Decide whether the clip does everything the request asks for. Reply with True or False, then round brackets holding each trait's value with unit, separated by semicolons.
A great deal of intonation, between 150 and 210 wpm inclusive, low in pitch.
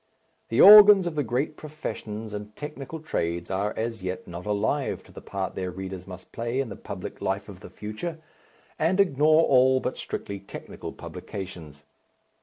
True (7.9 semitones; 170 wpm; 110 Hz)